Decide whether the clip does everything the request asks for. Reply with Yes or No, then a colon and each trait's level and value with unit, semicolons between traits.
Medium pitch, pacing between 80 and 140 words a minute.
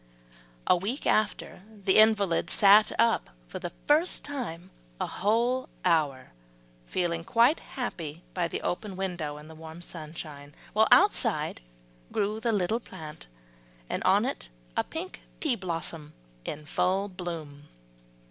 Yes: medium, 180 Hz; slow, 135 wpm